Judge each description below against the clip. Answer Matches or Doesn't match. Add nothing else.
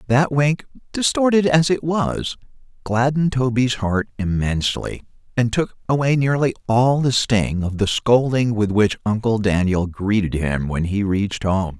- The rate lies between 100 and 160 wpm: Matches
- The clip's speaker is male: Matches